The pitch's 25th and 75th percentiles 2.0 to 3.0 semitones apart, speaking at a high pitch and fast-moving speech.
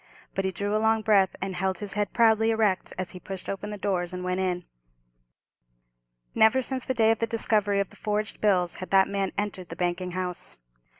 Yes: average, 2.7 semitones; high, 195 Hz; fast, 215 wpm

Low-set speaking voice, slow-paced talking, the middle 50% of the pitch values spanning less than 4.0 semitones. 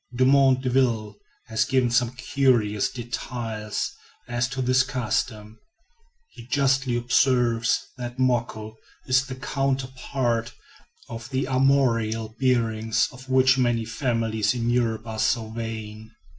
Yes: low, 120 Hz; slow, 115 wpm; narrow, 2.6 semitones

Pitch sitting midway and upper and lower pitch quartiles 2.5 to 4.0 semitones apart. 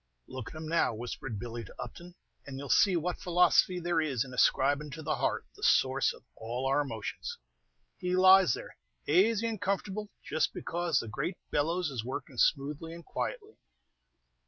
No: medium, 160 Hz; average, 5.2 semitones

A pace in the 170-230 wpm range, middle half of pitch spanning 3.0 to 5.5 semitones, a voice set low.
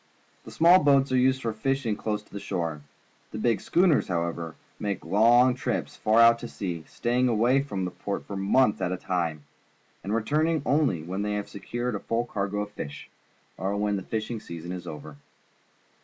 Yes: average, 185 wpm; average, 4.9 semitones; low, 105 Hz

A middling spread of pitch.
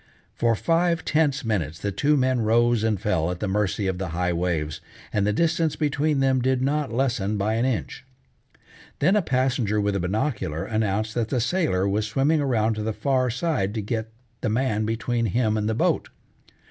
Yes: average, 4.5 semitones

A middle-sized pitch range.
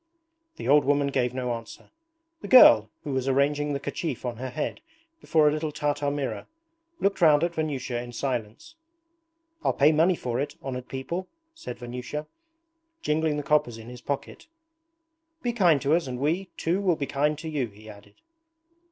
Yes: average, 3.7 semitones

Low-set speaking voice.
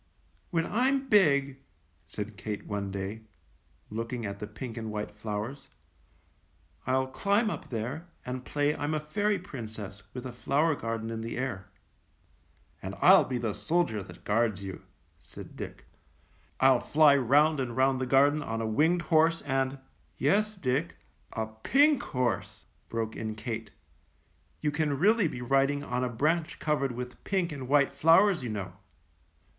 Yes: low, 130 Hz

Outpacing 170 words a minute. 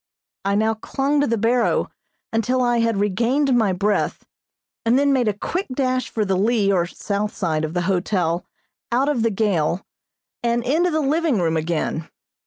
Yes: average, 180 wpm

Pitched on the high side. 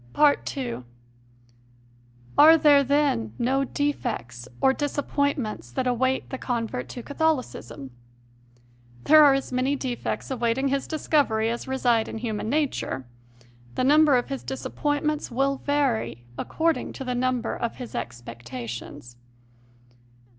Yes: very high, 255 Hz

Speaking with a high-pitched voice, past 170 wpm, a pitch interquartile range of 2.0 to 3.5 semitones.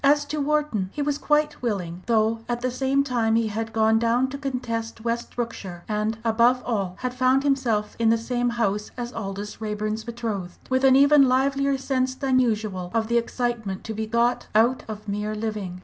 Yes: high, 235 Hz; average, 195 wpm; average, 3.2 semitones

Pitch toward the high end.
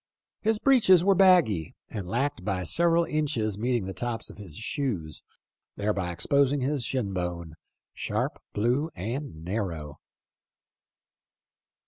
No: low, 115 Hz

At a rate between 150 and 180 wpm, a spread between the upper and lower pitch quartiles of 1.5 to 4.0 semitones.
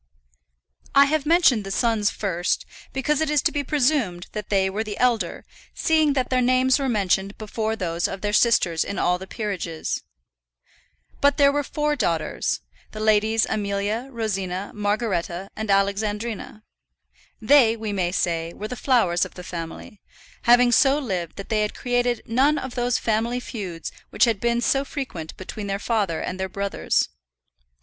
No: average, 165 wpm; average, 4.4 semitones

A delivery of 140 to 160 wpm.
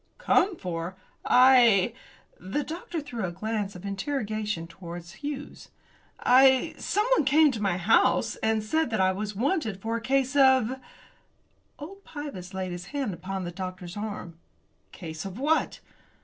Yes: average, 155 wpm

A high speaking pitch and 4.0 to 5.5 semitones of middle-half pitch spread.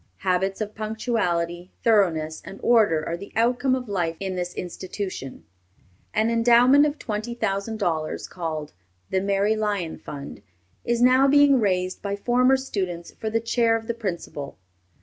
Yes: high, 205 Hz; average, 4.7 semitones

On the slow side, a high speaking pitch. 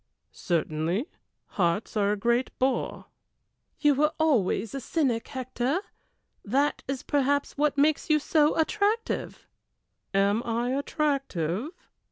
Yes: slow, 115 wpm; very high, 265 Hz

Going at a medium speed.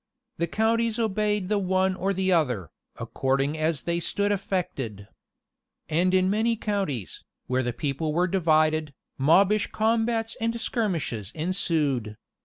No: slow, 130 wpm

